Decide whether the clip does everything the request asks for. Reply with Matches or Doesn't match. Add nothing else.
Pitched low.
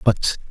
Matches